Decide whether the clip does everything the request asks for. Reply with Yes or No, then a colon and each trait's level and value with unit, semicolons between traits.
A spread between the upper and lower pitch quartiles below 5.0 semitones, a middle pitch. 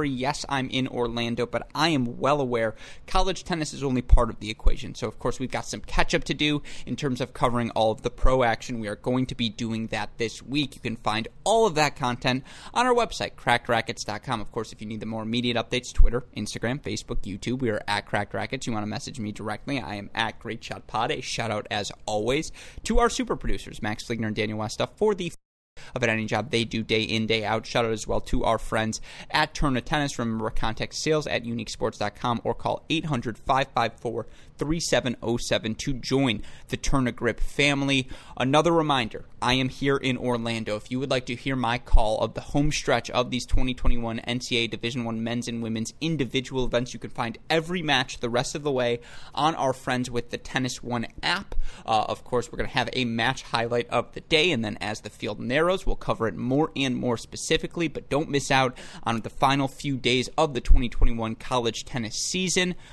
No: average, 3.3 semitones; low, 120 Hz